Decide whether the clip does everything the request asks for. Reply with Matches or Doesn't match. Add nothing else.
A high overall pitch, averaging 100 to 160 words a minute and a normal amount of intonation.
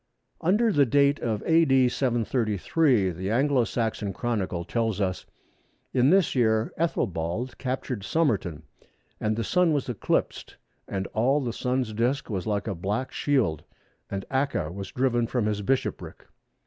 Doesn't match